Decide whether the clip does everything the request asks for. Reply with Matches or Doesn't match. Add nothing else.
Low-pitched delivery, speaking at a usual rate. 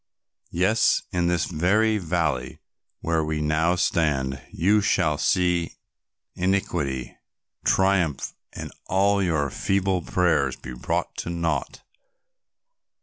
Doesn't match